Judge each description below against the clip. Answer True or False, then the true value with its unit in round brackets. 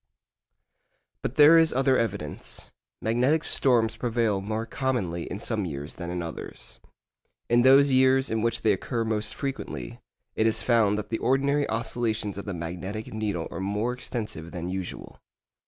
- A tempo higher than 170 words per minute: False (155 wpm)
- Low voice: True (110 Hz)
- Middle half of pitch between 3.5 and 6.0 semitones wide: True (4.5 semitones)